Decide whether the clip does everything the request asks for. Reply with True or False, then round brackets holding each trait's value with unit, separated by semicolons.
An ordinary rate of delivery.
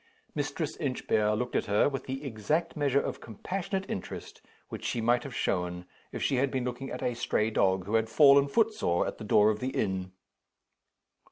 True (190 wpm)